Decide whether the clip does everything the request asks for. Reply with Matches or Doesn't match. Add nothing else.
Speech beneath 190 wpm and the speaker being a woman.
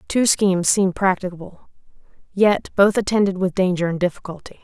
Matches